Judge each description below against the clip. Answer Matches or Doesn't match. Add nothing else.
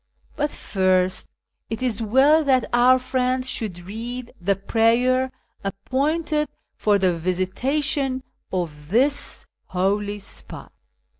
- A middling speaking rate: Doesn't match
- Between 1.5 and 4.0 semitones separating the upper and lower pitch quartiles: Doesn't match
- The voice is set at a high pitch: Matches